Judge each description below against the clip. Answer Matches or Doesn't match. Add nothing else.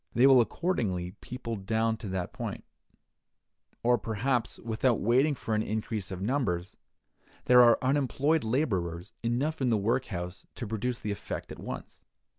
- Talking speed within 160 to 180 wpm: Doesn't match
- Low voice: Matches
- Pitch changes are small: Doesn't match